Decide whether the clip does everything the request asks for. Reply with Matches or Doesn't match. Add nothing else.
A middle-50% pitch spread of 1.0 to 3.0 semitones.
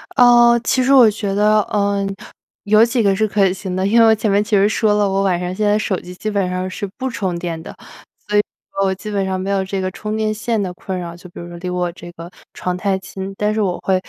Matches